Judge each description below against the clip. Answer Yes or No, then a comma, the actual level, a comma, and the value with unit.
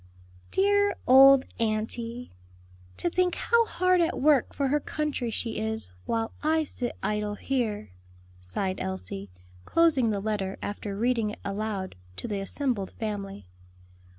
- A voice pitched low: No, high, 225 Hz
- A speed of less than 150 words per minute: Yes, slow, 135 wpm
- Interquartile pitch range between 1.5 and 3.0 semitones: No, wide, 5.6 semitones